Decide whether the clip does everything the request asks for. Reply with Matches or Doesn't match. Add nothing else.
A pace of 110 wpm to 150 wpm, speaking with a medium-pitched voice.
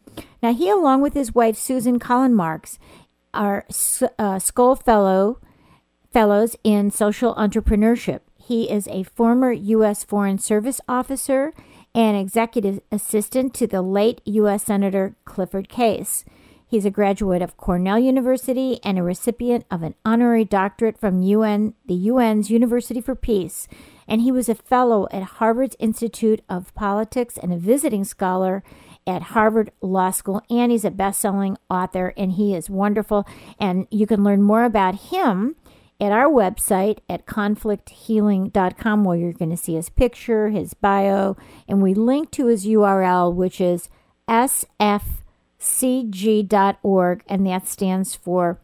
Doesn't match